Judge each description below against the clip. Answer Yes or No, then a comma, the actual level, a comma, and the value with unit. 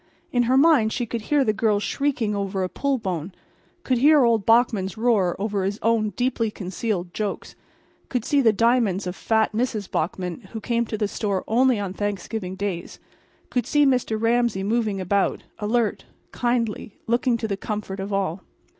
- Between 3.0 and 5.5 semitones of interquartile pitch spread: Yes, average, 3.4 semitones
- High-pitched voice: Yes, high, 220 Hz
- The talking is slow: No, average, 175 wpm